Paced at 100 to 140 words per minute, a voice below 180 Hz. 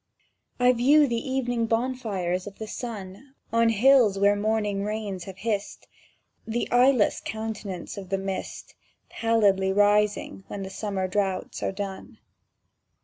No: slow, 135 wpm; high, 210 Hz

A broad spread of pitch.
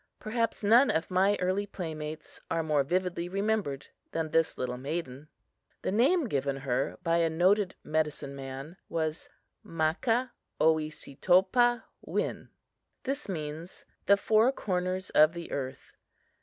No: average, 4.8 semitones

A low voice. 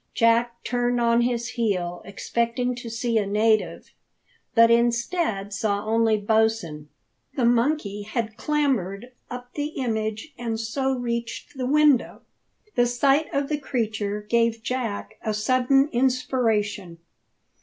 No: high, 235 Hz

